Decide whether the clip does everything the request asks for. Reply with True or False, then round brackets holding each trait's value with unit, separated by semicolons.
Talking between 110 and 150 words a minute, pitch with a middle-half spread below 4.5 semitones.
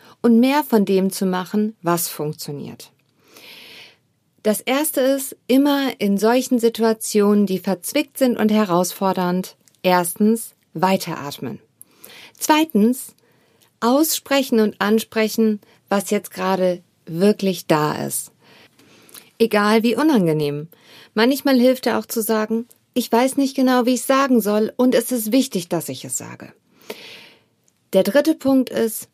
False (130 wpm; 4.9 semitones)